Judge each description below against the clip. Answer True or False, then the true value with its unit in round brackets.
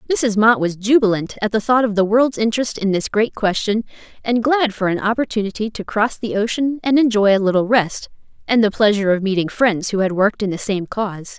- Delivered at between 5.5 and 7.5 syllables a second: True (5.7 syllables/s)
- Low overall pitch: False (215 Hz)